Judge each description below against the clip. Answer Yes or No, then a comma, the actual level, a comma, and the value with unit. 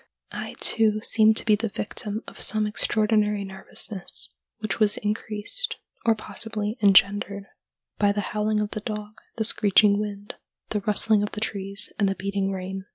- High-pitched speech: Yes, high, 210 Hz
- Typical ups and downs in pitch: No, narrow, 1.2 semitones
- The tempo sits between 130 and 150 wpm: No, average, 160 wpm